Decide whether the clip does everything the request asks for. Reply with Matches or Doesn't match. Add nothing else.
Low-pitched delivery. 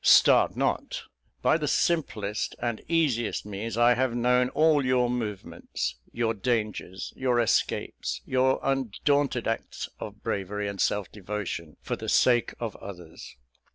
Matches